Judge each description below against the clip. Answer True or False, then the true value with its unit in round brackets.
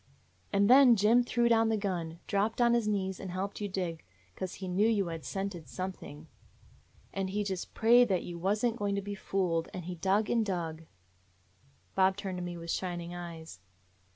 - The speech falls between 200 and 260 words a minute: True (205 wpm)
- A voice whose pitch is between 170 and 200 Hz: True (190 Hz)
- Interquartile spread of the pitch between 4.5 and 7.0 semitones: False (3.3 semitones)